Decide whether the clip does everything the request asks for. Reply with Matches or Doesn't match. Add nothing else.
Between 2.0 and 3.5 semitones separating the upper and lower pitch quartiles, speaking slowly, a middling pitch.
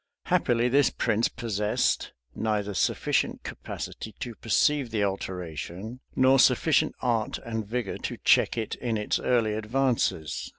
Doesn't match